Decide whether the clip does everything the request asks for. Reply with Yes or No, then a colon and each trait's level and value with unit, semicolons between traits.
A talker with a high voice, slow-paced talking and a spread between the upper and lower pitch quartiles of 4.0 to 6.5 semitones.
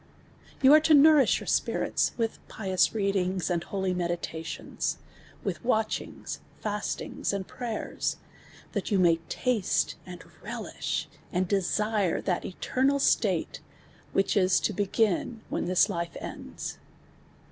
No: high, 195 Hz; slow, 130 wpm; average, 3.6 semitones